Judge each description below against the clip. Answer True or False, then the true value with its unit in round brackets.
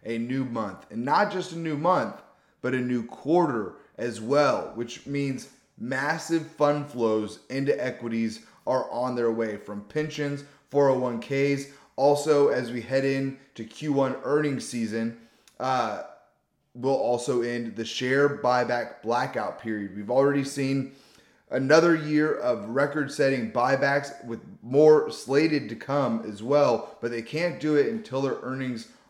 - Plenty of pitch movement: False (3.6 semitones)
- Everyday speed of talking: True (145 wpm)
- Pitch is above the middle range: False (135 Hz)